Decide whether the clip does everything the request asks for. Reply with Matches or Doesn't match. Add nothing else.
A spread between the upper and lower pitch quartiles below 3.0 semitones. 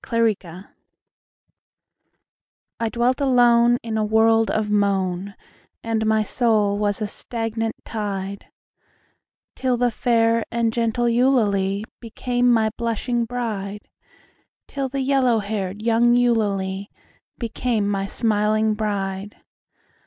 Matches